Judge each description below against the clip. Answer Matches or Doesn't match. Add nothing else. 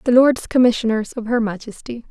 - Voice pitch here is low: Doesn't match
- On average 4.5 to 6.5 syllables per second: Matches